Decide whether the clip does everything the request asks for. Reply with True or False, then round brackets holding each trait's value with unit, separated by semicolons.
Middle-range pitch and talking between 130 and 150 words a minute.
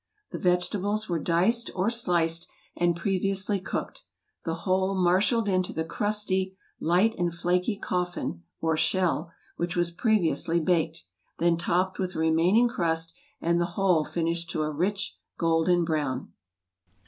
True (175 Hz; 140 wpm)